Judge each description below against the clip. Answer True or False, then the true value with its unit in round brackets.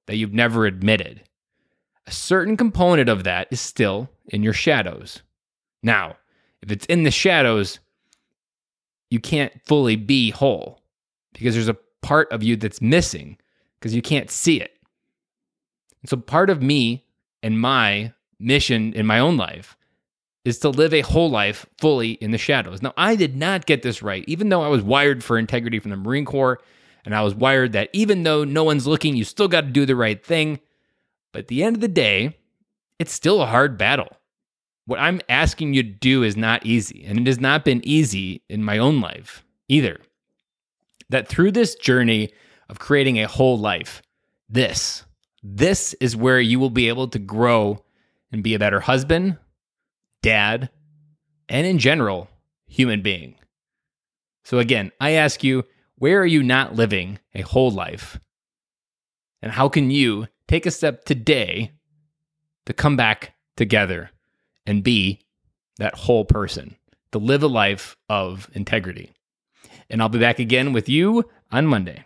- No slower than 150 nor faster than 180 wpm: True (170 wpm)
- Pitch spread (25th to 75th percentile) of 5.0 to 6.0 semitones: True (5.4 semitones)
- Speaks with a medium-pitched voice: False (125 Hz)